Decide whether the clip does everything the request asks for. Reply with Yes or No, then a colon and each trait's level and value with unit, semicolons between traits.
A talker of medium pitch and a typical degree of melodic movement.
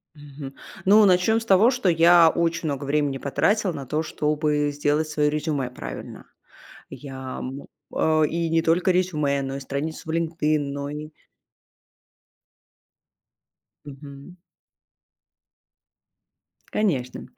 Yes: medium, 150 Hz; average, 3.2 semitones